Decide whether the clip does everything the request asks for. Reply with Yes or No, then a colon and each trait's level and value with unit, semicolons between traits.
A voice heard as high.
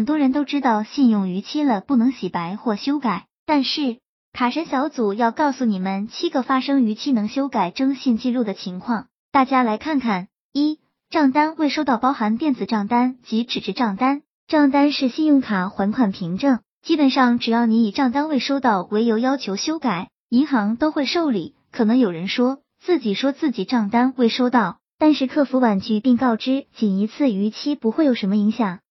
Yes: very high, 250 Hz